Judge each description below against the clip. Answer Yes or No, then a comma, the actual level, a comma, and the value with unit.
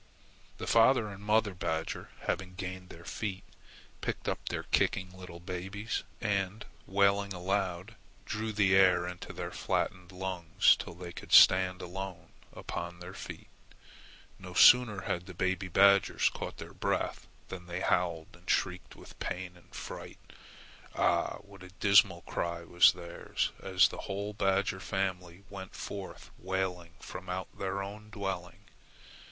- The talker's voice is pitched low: Yes, very low, 95 Hz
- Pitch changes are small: Yes, narrow, 1.9 semitones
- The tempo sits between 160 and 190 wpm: No, average, 145 wpm